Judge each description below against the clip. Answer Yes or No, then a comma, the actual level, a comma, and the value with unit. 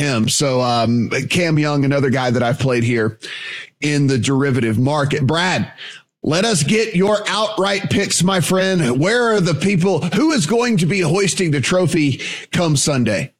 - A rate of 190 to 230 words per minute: No, average, 170 wpm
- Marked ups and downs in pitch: Yes, wide, 5.9 semitones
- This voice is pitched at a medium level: Yes, medium, 160 Hz